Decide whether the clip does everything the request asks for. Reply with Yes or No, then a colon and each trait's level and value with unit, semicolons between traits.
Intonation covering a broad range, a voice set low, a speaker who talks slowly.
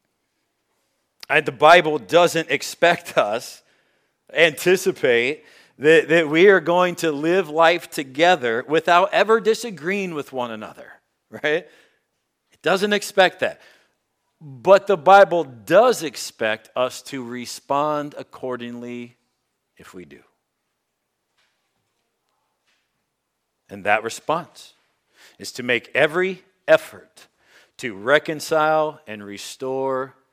No: wide, 6.2 semitones; medium, 160 Hz; slow, 100 wpm